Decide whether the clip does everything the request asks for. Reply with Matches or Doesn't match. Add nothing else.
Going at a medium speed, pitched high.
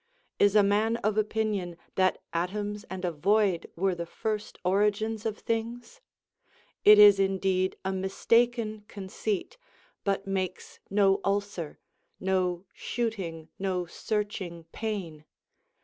Doesn't match